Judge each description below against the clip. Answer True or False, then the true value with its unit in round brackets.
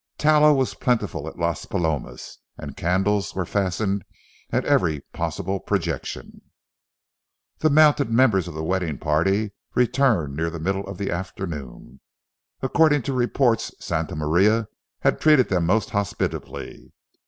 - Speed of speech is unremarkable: False (130 wpm)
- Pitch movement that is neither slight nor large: False (6.5 semitones)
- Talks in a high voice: False (95 Hz)